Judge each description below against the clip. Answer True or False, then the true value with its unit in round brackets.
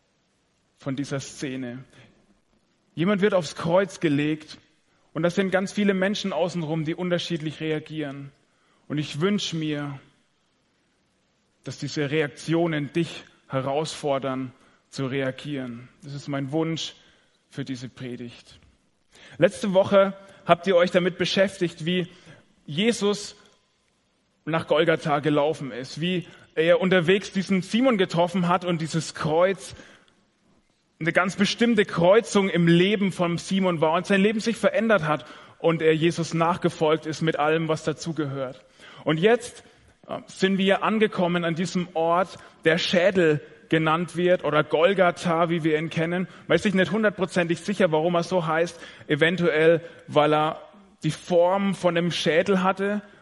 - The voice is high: False (170 Hz)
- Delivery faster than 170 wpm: False (135 wpm)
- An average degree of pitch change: True (3.5 semitones)